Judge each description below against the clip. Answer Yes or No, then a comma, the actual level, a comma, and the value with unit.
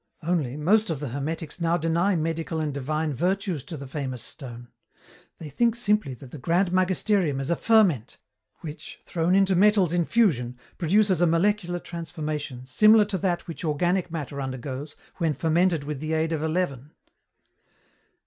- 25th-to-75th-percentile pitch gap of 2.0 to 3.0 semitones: No, average, 4.1 semitones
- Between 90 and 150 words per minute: No, average, 165 wpm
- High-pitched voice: No, medium, 165 Hz